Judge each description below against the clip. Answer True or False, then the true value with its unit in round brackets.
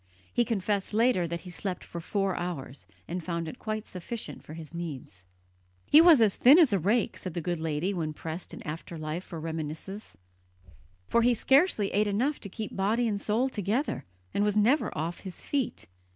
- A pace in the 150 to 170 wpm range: False (195 wpm)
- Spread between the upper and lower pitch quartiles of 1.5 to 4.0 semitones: False (5.1 semitones)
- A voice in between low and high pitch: False (195 Hz)